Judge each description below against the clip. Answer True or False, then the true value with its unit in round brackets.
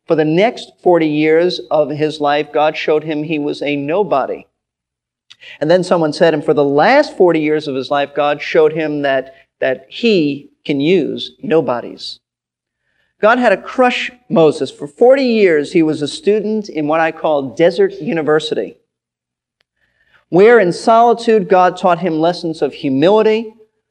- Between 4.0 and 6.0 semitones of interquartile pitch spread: True (5.6 semitones)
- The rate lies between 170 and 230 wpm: False (160 wpm)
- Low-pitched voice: False (160 Hz)